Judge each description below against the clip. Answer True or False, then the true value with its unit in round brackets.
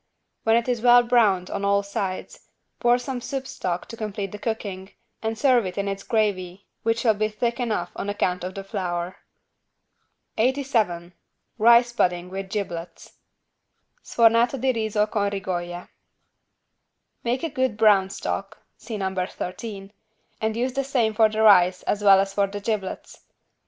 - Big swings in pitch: False (3.5 semitones)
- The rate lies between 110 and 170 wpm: True (160 wpm)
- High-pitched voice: True (210 Hz)